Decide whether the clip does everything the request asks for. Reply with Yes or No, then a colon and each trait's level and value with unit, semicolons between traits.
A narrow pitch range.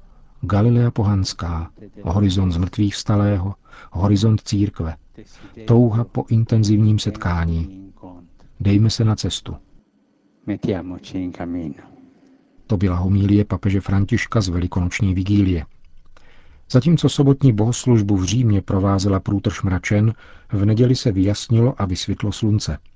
No: average, 3.1 semitones